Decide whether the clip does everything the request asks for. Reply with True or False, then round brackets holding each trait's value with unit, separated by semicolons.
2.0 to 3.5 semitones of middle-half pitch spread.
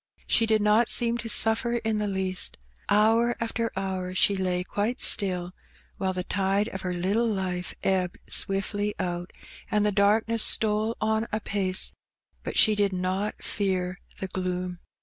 True (2.8 semitones)